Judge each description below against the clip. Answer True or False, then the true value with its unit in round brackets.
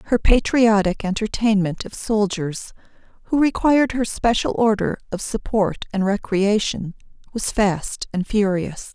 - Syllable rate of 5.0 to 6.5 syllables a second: False (4.3 syllables/s)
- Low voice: False (210 Hz)